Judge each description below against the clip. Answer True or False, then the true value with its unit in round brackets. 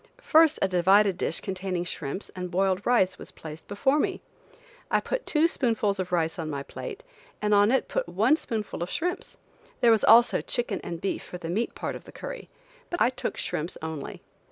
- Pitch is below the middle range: False (200 Hz)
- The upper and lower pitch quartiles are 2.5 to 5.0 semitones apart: False (5.4 semitones)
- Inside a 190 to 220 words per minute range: True (200 wpm)